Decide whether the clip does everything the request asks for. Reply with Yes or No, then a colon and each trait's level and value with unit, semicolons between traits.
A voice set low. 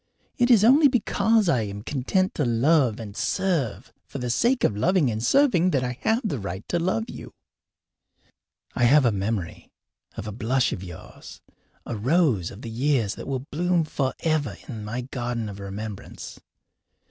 Yes: low, 125 Hz